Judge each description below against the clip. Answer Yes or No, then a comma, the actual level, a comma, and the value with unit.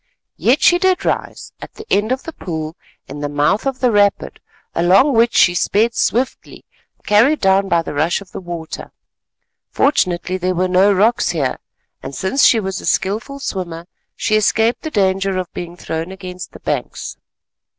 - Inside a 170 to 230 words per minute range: Yes, average, 175 wpm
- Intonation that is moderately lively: Yes, average, 4.7 semitones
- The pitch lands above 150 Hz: Yes, high, 190 Hz